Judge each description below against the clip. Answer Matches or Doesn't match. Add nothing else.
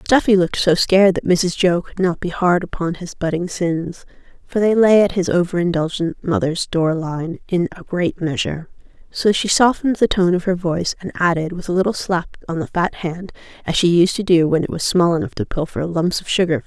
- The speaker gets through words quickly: Matches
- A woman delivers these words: Matches